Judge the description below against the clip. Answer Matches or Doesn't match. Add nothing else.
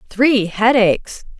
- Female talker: Matches